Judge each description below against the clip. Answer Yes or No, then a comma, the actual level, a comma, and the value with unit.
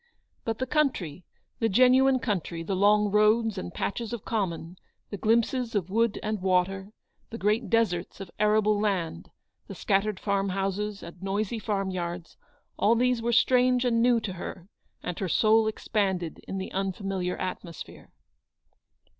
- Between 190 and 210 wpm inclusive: No, average, 155 wpm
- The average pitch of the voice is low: No, high, 205 Hz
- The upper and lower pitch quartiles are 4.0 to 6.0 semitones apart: No, average, 3.4 semitones